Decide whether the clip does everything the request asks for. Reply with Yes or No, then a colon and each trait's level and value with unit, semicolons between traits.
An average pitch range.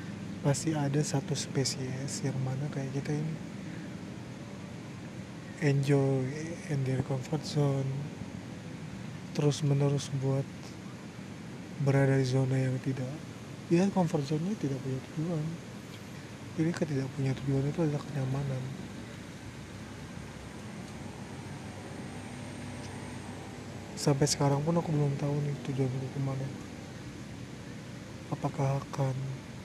No: narrow, 2.1 semitones